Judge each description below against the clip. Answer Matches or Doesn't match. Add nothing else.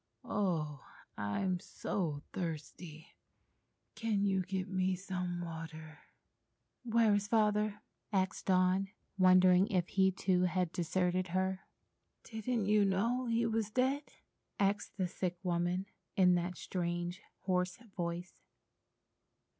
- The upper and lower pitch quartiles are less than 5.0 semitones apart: Matches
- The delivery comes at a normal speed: Doesn't match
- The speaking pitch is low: Doesn't match